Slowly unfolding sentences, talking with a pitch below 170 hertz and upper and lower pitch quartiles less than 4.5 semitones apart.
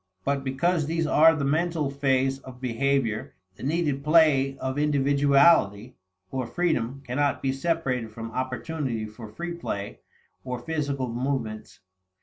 Yes: slow, 130 wpm; low, 135 Hz; average, 3.2 semitones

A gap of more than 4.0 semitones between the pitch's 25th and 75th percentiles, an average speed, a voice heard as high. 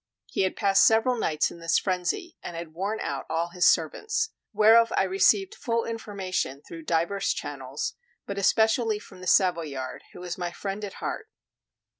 Yes: average, 4.4 semitones; average, 170 wpm; high, 195 Hz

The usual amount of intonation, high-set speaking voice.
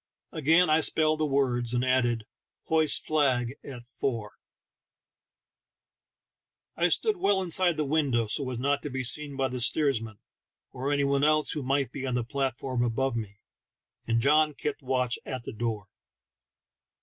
No: average, 3.8 semitones; low, 135 Hz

